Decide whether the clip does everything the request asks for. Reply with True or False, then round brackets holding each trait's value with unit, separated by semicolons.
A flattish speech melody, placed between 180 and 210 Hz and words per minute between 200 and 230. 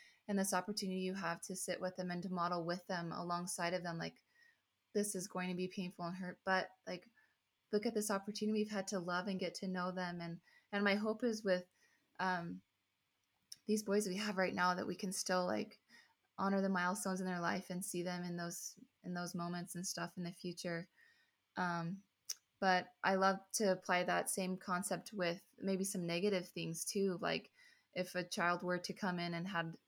True (1.8 semitones; 185 Hz; 205 wpm)